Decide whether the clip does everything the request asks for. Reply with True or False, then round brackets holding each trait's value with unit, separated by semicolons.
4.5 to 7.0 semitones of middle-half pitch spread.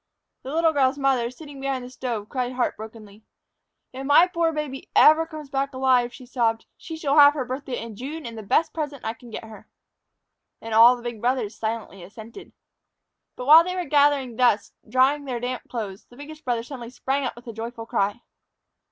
False (3.8 semitones)